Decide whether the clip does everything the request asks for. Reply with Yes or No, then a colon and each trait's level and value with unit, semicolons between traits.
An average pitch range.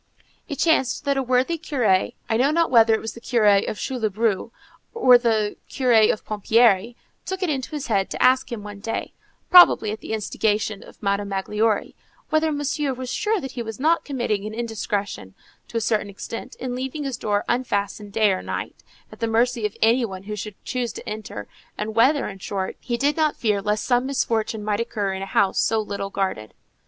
Yes: average, 3.8 semitones